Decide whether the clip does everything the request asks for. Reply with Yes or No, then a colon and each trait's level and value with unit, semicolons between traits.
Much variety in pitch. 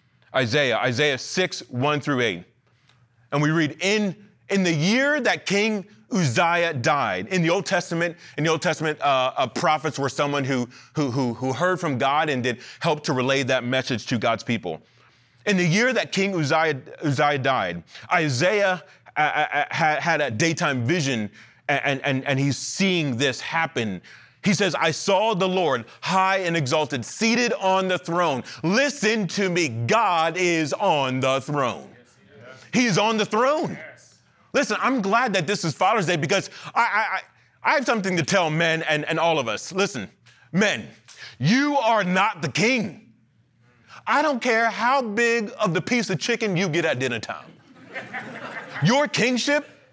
Yes: wide, 6.5 semitones